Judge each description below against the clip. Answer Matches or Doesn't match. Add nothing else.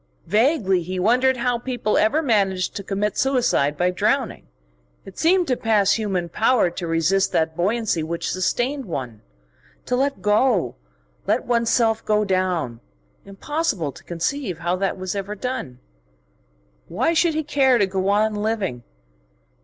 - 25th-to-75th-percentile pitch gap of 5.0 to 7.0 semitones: Matches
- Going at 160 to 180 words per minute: Doesn't match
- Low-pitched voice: Doesn't match